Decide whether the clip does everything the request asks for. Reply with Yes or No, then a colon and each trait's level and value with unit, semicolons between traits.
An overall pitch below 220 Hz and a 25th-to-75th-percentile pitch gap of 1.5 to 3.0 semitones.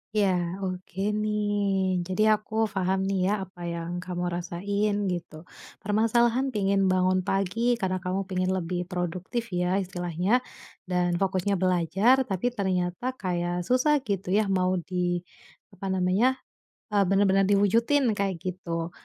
Yes: high, 190 Hz; narrow, 2.4 semitones